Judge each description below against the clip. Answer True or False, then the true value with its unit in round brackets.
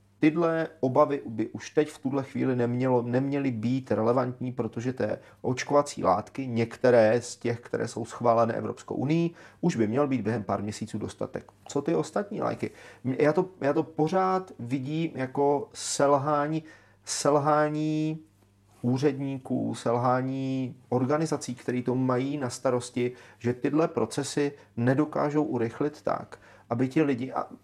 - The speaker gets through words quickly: False (135 wpm)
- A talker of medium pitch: False (130 Hz)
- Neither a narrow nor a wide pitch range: True (3.8 semitones)